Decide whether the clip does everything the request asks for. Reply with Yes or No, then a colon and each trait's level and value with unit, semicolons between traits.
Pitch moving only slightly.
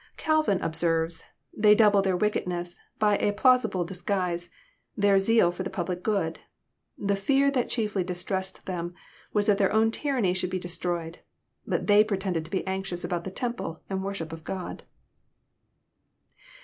No: average, 3.0 semitones